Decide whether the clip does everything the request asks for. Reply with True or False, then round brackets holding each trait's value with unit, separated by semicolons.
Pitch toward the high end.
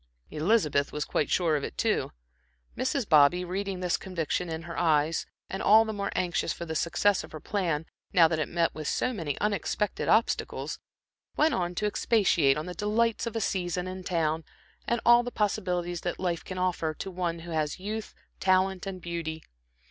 False (180 Hz)